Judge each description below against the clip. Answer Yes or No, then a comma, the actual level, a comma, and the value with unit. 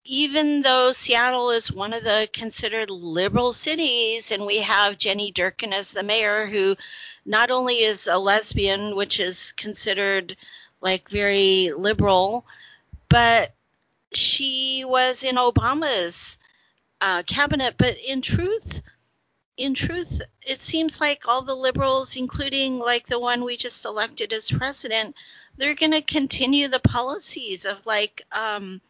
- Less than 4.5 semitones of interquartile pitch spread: No, average, 4.8 semitones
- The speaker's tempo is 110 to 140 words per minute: Yes, slow, 135 wpm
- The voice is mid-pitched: No, high, 235 Hz